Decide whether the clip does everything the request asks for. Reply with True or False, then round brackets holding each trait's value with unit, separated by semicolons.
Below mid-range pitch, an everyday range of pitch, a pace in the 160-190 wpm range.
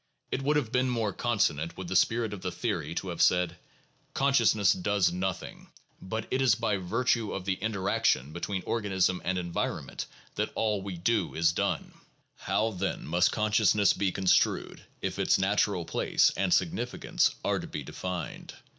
True (95 Hz; 3.7 semitones; 170 wpm)